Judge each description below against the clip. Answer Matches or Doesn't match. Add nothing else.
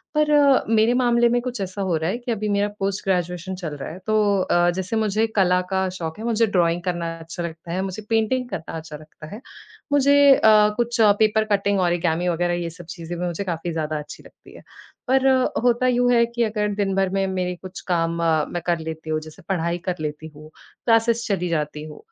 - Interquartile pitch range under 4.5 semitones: Doesn't match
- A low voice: Doesn't match